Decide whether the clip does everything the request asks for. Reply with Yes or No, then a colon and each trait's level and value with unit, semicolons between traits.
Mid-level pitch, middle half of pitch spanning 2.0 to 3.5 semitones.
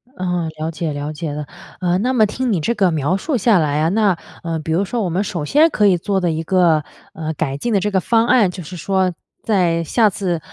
No: medium, 180 Hz; average, 4.4 semitones